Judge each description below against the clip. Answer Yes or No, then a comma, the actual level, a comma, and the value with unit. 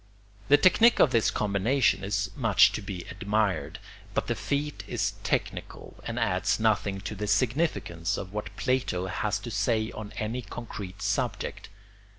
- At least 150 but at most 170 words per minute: Yes, average, 155 wpm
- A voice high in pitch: No, low, 105 Hz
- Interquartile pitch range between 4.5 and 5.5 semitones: No, average, 3.6 semitones